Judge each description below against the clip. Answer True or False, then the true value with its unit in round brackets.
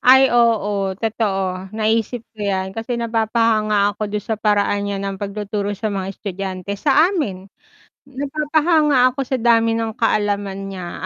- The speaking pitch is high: True (215 Hz)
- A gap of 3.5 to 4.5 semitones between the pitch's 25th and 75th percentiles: False (3.0 semitones)